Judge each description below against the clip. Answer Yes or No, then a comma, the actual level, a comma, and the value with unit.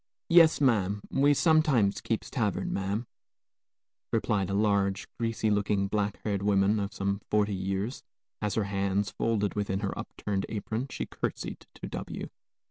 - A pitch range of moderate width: No, narrow, 2.0 semitones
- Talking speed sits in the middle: Yes, average, 150 wpm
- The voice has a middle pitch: No, low, 105 Hz